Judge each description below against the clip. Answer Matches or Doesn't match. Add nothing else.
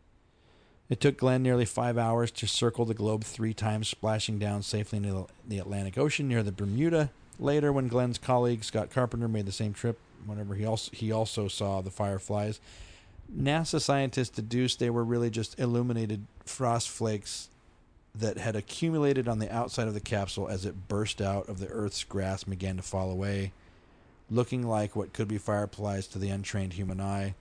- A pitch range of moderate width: Matches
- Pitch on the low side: Matches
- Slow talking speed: Doesn't match